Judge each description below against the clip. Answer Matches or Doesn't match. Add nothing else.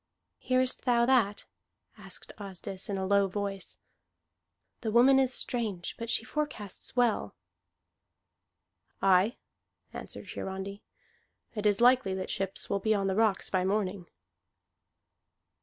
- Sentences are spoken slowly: Matches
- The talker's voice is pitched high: Matches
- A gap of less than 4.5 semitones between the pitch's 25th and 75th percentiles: Matches